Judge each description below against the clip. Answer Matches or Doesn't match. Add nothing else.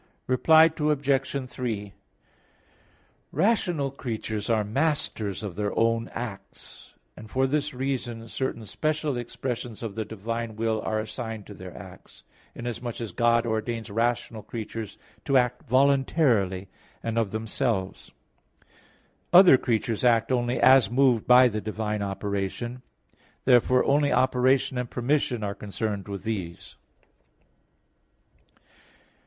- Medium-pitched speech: Doesn't match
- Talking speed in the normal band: Doesn't match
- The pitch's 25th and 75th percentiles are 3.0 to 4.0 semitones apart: Matches